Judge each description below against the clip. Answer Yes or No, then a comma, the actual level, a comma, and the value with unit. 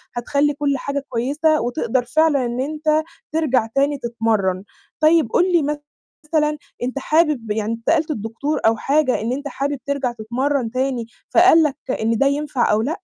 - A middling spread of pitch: Yes, average, 4.2 semitones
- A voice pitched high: Yes, very high, 275 Hz